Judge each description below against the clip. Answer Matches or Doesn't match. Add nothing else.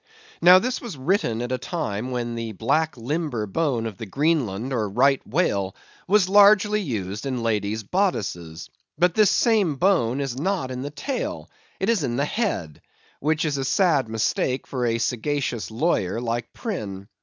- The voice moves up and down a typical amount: Doesn't match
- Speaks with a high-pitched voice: Doesn't match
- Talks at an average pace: Matches